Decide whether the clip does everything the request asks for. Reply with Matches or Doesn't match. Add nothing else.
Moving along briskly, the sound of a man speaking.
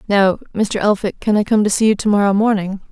Doesn't match